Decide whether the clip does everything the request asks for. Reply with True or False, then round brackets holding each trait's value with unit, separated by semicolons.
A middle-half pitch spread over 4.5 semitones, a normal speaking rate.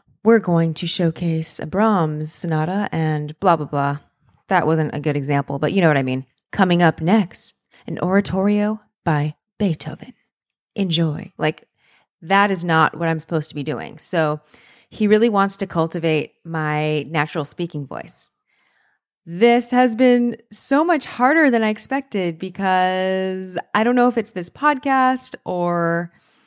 True (5.1 semitones; 155 wpm)